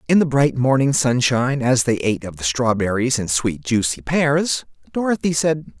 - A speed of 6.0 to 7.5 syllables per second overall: No, 4.9 syllables/s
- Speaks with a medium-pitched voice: No, low, 130 Hz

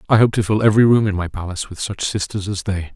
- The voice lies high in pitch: No, low, 100 Hz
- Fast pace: Yes, fast, 285 wpm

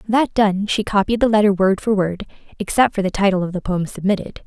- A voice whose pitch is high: Yes, high, 200 Hz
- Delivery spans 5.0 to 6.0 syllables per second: Yes, 5.7 syllables/s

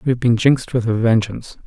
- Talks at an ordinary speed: No, fast, 250 wpm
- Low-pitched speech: Yes, low, 120 Hz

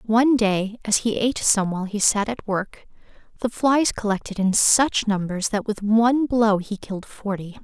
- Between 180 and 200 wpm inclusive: Yes, average, 190 wpm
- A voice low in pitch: No, high, 215 Hz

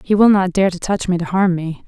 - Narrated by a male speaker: No, female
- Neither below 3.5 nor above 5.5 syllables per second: No, 5.7 syllables/s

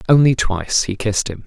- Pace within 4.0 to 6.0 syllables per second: No, 6.2 syllables/s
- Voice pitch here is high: No, low, 110 Hz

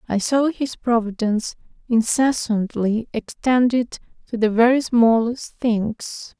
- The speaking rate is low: Yes, slow, 105 wpm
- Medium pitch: No, high, 230 Hz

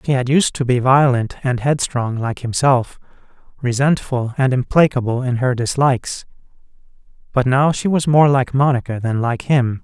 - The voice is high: No, low, 130 Hz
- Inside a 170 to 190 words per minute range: No, average, 160 wpm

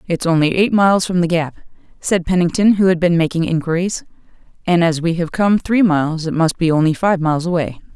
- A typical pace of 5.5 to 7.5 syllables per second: Yes, 5.9 syllables/s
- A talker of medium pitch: Yes, medium, 175 Hz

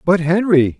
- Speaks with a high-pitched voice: No, medium, 170 Hz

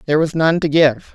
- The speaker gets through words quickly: Yes, fast, 260 wpm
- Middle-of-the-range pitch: Yes, medium, 155 Hz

